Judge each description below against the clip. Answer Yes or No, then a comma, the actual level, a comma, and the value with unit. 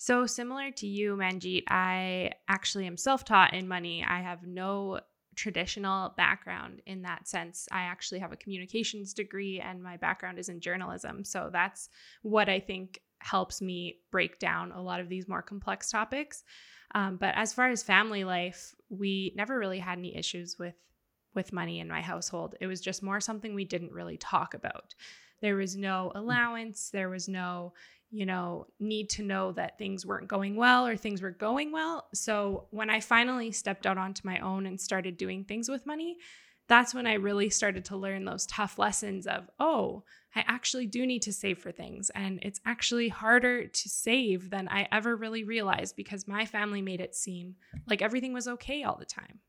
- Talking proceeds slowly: No, average, 190 wpm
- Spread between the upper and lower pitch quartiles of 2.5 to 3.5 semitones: Yes, average, 3.0 semitones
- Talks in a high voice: Yes, high, 200 Hz